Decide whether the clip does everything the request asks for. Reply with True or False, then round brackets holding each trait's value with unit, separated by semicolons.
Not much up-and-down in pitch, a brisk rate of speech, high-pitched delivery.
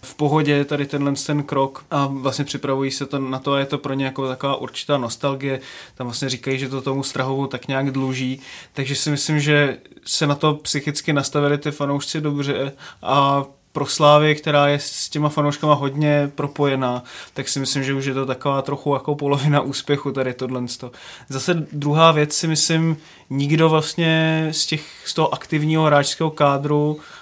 False (1.7 semitones; 185 wpm; 140 Hz)